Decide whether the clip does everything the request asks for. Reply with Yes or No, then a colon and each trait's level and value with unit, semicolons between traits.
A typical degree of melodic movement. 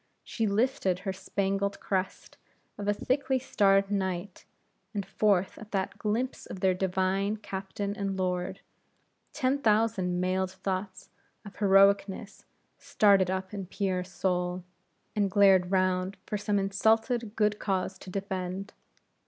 No: narrow, 1.7 semitones